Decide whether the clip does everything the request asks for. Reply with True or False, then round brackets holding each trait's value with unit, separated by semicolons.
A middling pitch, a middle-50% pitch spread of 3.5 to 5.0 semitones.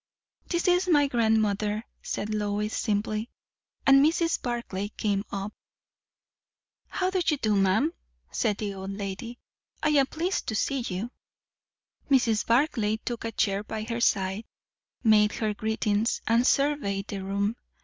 False (220 Hz; 4.4 semitones)